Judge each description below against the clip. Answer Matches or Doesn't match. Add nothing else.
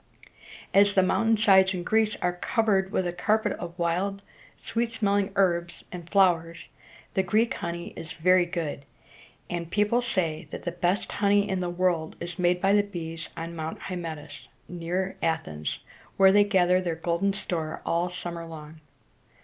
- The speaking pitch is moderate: Matches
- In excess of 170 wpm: Doesn't match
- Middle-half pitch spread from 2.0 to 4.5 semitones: Matches